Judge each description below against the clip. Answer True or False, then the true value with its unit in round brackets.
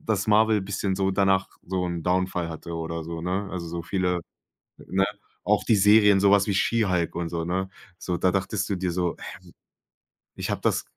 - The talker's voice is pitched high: False (95 Hz)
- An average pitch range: False (2.3 semitones)